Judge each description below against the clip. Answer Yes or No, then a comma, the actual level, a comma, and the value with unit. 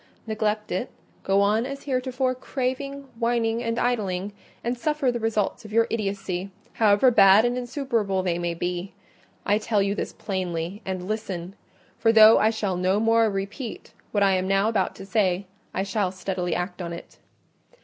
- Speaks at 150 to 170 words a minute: Yes, average, 165 wpm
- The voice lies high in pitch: Yes, high, 210 Hz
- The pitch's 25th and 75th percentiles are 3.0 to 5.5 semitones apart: Yes, average, 3.4 semitones